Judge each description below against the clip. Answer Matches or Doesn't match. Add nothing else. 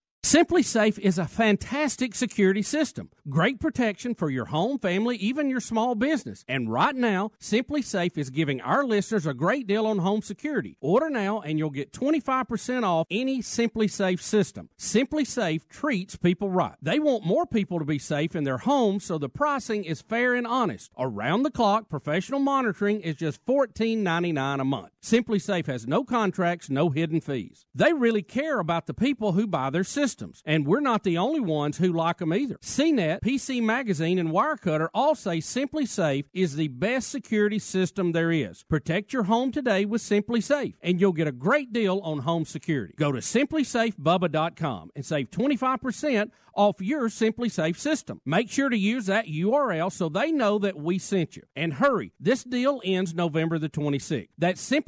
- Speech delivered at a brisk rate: Doesn't match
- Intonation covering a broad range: Matches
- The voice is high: Matches